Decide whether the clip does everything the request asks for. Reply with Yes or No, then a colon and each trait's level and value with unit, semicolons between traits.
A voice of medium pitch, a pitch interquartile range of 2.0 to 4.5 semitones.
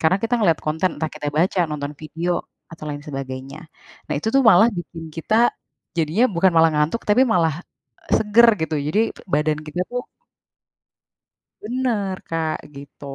No: medium, 165 Hz; average, 5.2 semitones